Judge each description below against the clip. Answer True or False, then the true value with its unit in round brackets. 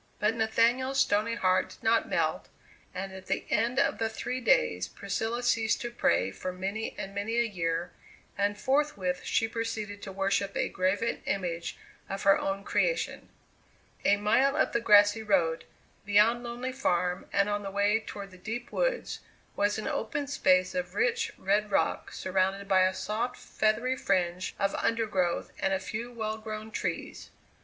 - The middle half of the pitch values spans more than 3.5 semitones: False (3.2 semitones)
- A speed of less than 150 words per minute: False (165 wpm)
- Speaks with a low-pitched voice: False (210 Hz)